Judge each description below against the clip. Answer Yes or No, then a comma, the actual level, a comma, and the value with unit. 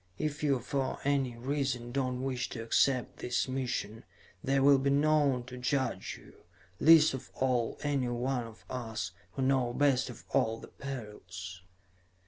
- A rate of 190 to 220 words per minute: No, average, 160 wpm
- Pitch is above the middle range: No, low, 130 Hz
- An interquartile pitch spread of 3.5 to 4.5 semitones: No, narrow, 2.4 semitones